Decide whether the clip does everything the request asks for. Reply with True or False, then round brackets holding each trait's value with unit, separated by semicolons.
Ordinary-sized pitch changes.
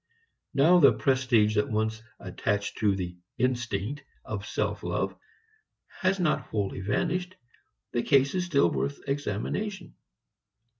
False (6.7 semitones)